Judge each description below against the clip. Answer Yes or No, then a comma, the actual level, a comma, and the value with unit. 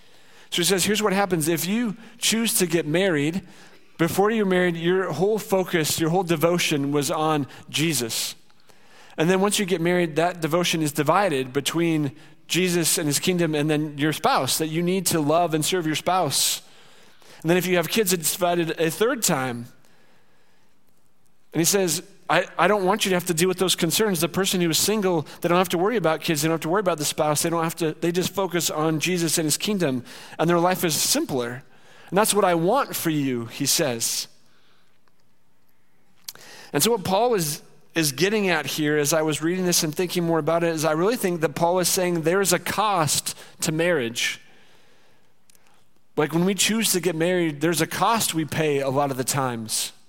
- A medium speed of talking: No, fast, 210 wpm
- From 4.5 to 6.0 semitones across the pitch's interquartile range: No, average, 2.9 semitones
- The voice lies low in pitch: No, medium, 170 Hz